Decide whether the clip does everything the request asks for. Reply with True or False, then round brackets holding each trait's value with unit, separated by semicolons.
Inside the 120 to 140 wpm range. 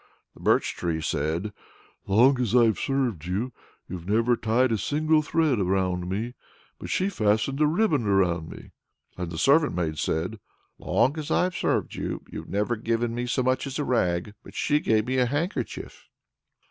False (175 wpm)